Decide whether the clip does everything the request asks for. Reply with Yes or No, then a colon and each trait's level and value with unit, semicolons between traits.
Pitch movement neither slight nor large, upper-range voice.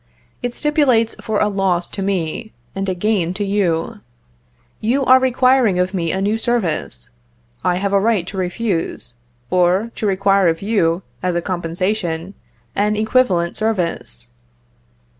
Yes: average, 3.9 semitones; high, 195 Hz